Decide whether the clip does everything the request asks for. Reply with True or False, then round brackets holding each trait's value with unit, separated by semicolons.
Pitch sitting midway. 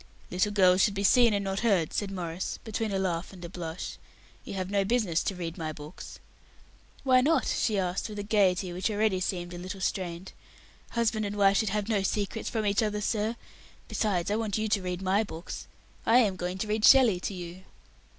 False (195 Hz)